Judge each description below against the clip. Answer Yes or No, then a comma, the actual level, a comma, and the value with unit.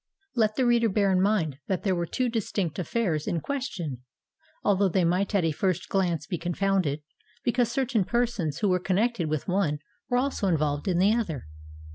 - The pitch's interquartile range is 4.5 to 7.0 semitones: Yes, average, 5.0 semitones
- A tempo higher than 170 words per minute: Yes, average, 185 wpm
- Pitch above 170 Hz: Yes, high, 190 Hz